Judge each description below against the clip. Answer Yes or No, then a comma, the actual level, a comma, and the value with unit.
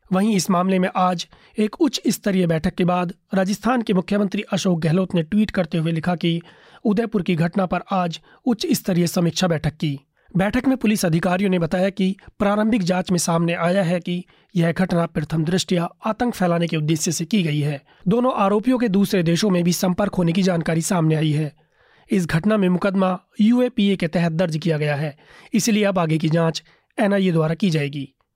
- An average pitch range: Yes, average, 3.2 semitones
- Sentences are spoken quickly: Yes, fast, 195 wpm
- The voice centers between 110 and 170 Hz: No, medium, 185 Hz